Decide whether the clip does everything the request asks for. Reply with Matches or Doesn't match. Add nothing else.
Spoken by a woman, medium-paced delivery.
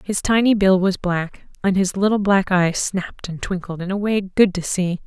Doesn't match